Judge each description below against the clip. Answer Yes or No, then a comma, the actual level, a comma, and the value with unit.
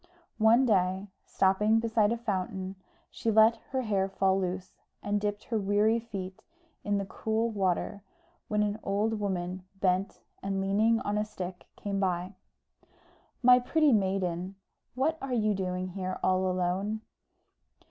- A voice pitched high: Yes, high, 200 Hz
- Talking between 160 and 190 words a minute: No, average, 145 wpm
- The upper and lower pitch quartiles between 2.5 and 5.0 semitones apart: Yes, average, 2.8 semitones